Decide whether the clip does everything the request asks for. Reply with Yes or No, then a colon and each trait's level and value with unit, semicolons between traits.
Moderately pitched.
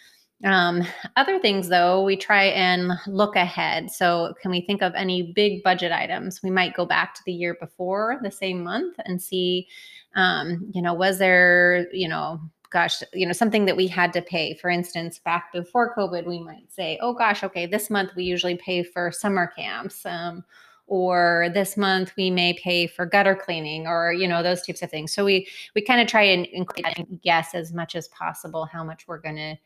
Yes: medium, 180 Hz